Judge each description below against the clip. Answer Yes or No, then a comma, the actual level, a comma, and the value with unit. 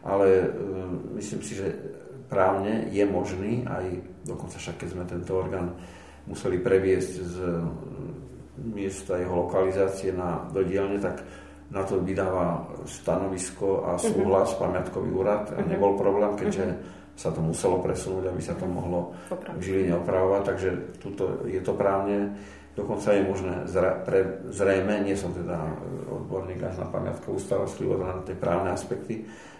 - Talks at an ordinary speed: Yes, average, 140 wpm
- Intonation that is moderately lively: No, narrow, 1.5 semitones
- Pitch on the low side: Yes, very low, 95 Hz